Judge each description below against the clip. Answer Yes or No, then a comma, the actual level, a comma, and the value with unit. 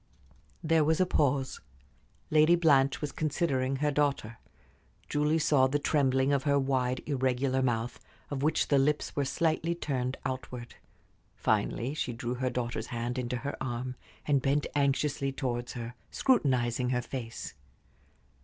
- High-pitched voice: No, low, 135 Hz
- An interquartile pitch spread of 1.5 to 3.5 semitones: Yes, average, 2.8 semitones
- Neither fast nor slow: Yes, average, 145 wpm